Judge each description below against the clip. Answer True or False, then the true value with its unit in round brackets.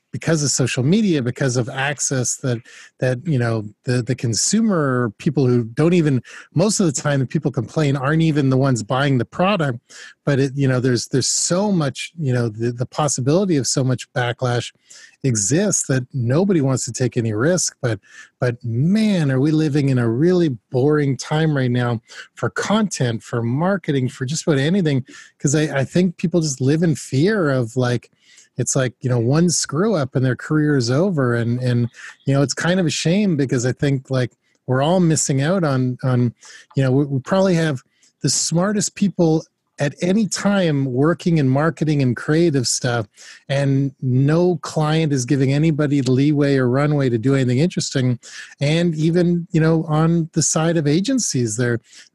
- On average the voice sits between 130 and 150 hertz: True (140 Hz)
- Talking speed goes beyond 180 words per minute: True (190 wpm)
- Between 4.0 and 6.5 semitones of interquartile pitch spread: True (4.3 semitones)